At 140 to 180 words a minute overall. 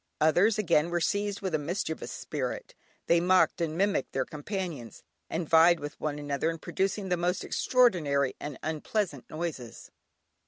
Yes: average, 155 wpm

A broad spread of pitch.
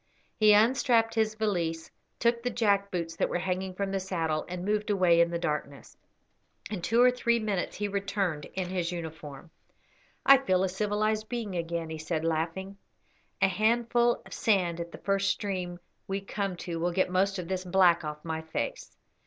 No: average, 3.8 semitones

